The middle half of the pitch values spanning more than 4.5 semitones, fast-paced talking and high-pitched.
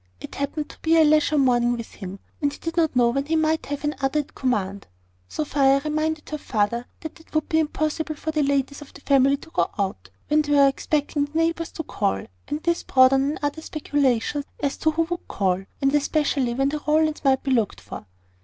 No: average, 2.8 semitones; fast, 220 wpm; very high, 290 Hz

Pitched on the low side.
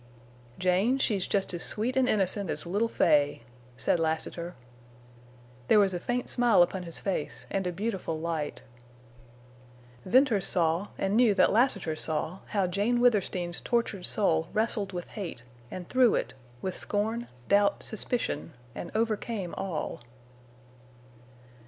No: high, 195 Hz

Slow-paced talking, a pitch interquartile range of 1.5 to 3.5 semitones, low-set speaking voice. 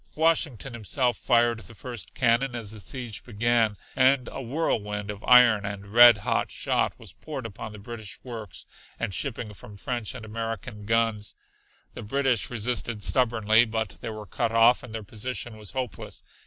No: average, 170 wpm; average, 2.7 semitones; low, 115 Hz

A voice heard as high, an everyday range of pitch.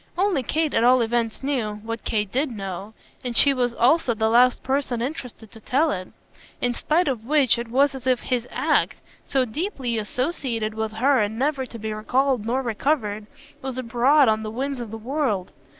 Yes: high, 245 Hz; average, 3.6 semitones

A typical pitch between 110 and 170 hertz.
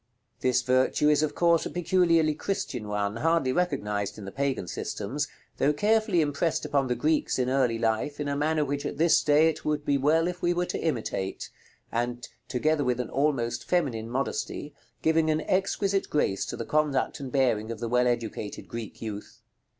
Yes: medium, 140 Hz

